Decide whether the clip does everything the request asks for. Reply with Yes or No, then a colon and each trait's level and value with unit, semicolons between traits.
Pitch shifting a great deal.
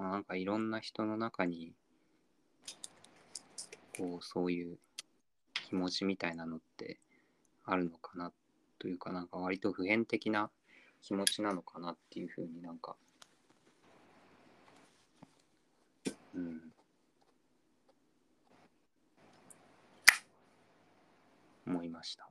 No: narrow, 2.6 semitones